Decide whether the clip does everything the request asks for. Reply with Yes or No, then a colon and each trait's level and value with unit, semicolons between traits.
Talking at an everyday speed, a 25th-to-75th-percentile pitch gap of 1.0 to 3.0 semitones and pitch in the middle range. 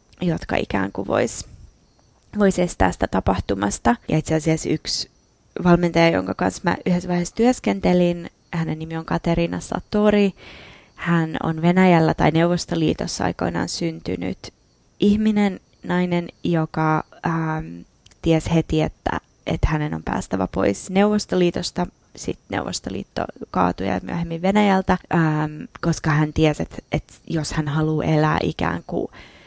Yes: average, 125 wpm; narrow, 2.5 semitones; medium, 160 Hz